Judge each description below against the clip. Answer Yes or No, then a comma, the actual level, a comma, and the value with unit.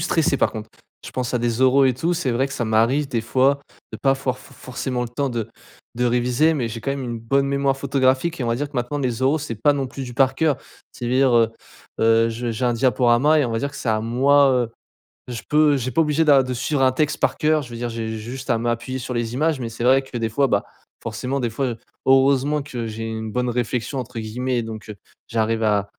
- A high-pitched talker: No, low, 125 Hz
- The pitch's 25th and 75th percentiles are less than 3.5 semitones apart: Yes, average, 3.0 semitones